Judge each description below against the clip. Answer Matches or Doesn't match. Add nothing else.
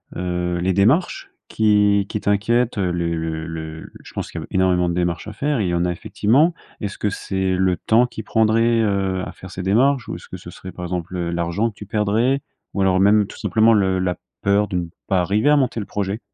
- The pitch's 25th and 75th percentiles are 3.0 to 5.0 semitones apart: Matches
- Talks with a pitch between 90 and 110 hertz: Matches